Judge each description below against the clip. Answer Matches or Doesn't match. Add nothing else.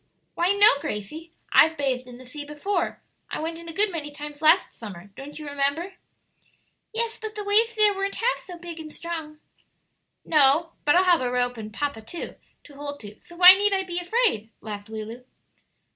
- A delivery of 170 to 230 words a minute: Matches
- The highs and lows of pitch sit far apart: Matches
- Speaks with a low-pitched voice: Doesn't match